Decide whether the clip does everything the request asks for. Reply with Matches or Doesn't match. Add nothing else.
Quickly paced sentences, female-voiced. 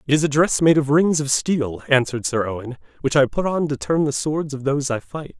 Doesn't match